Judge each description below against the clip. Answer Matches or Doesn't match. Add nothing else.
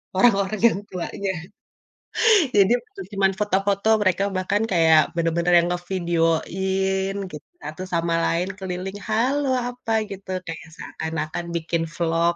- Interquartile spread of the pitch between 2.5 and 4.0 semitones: Matches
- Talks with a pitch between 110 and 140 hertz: Doesn't match